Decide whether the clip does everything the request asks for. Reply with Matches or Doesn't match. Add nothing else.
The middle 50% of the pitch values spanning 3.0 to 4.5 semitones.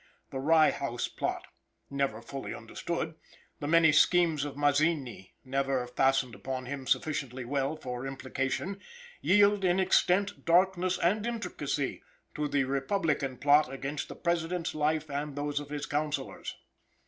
Matches